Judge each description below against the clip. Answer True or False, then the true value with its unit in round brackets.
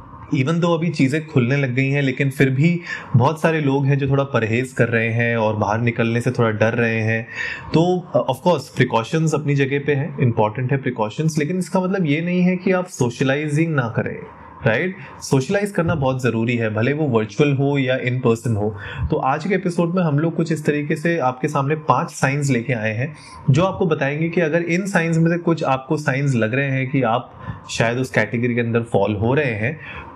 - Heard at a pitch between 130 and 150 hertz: True (140 Hz)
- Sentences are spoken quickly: True (220 wpm)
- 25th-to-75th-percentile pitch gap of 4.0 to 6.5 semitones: True (5.0 semitones)